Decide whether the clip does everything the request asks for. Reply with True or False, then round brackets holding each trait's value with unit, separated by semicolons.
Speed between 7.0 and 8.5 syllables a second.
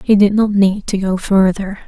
False (4.7 syllables/s)